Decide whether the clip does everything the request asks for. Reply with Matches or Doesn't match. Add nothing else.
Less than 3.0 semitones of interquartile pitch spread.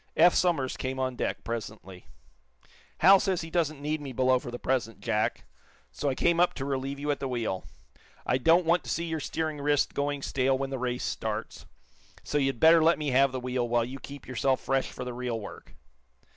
Doesn't match